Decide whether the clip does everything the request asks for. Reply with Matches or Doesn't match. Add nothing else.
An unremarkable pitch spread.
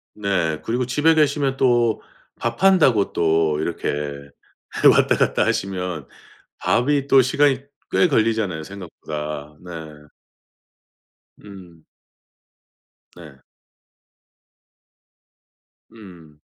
Doesn't match